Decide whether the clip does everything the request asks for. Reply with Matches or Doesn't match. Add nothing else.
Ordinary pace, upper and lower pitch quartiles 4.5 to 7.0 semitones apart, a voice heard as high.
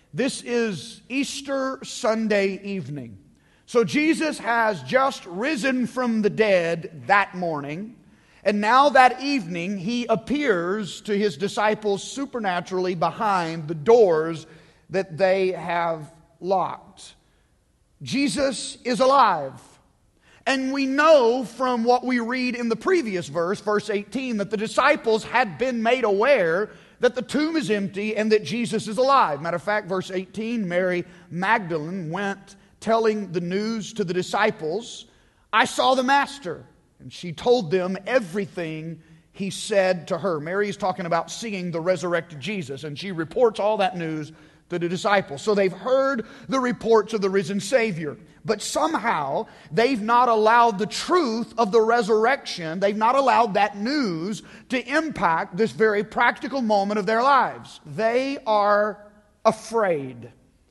Matches